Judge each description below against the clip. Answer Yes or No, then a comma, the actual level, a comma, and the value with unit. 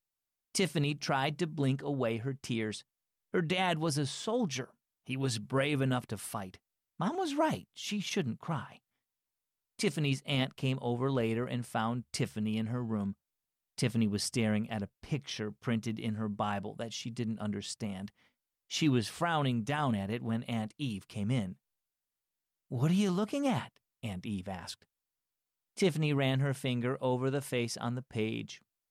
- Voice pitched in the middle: No, low, 125 Hz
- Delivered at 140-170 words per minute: Yes, average, 160 wpm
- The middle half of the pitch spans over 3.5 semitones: Yes, average, 4.4 semitones